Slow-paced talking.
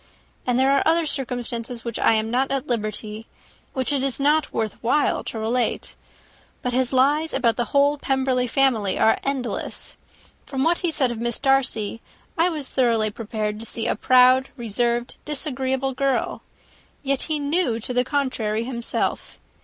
No: average, 165 wpm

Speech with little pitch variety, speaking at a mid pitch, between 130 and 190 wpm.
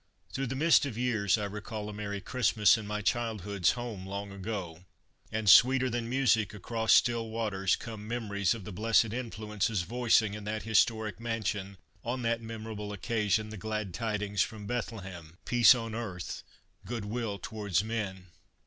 No: narrow, 2.3 semitones; low, 110 Hz; average, 165 wpm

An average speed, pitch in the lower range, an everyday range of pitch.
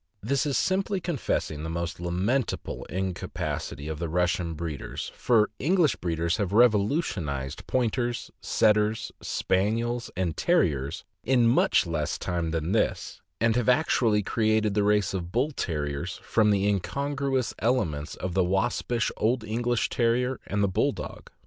No: average, 145 wpm; low, 105 Hz; wide, 5.9 semitones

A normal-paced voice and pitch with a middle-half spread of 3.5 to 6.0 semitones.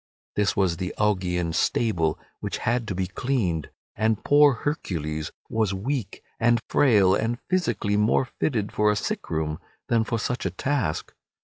Yes: average, 155 wpm; average, 4.5 semitones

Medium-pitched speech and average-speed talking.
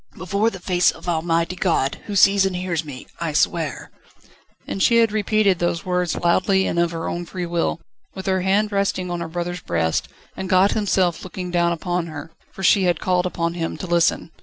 No: medium, 180 Hz; fast, 210 wpm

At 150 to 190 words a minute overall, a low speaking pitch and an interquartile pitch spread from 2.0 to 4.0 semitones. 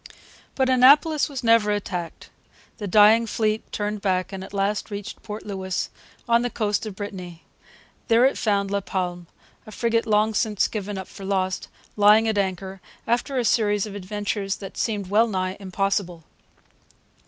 No: average, 160 wpm; high, 205 Hz; narrow, 2.5 semitones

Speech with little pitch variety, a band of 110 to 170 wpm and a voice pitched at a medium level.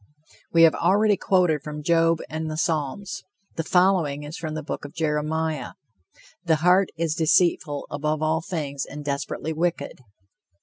Yes: narrow, 2.2 semitones; average, 150 wpm; medium, 160 Hz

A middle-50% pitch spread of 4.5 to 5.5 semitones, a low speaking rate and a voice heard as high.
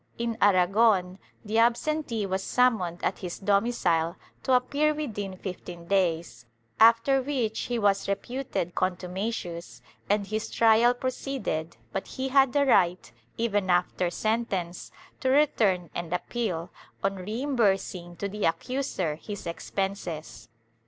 Yes: average, 5.0 semitones; slow, 125 wpm; high, 200 Hz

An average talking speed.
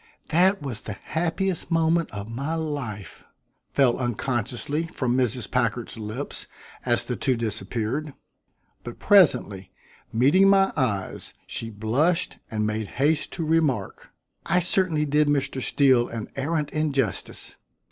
No: slow, 125 wpm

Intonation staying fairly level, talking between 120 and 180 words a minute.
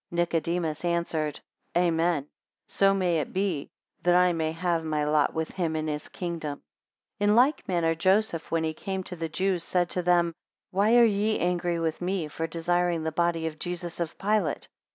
No: narrow, 2.1 semitones; average, 190 wpm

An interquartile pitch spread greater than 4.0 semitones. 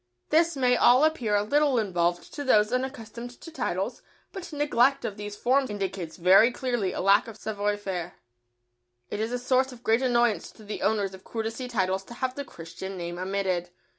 Yes: average, 4.7 semitones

